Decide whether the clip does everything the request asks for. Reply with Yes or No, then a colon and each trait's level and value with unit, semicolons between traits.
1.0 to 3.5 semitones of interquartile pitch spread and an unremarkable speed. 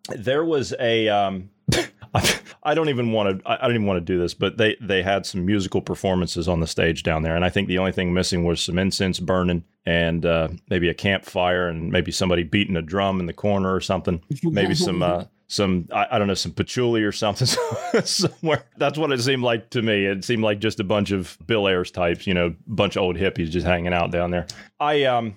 No: average, 3.1 semitones; fast, 235 wpm